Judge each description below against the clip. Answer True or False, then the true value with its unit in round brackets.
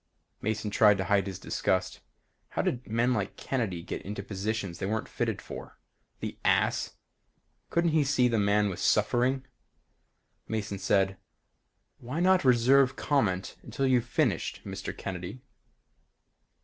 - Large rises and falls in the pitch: False (4.6 semitones)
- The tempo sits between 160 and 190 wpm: False (135 wpm)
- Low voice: True (110 Hz)